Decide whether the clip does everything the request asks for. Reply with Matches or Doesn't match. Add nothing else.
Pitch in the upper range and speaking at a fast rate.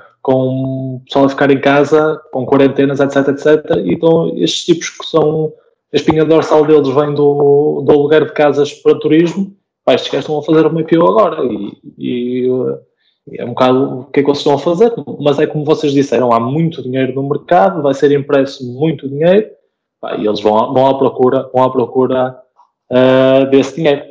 Doesn't match